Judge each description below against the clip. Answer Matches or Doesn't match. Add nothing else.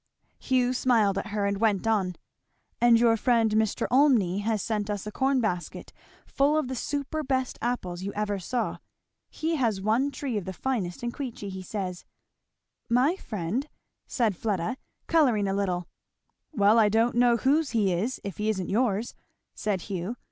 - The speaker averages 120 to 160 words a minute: Doesn't match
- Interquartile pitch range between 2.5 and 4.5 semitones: Matches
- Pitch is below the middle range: Doesn't match